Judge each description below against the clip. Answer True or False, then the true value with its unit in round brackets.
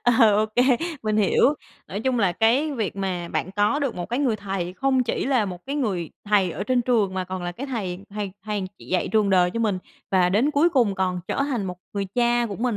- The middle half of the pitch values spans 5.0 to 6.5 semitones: False (4.5 semitones)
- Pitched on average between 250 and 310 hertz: False (210 Hz)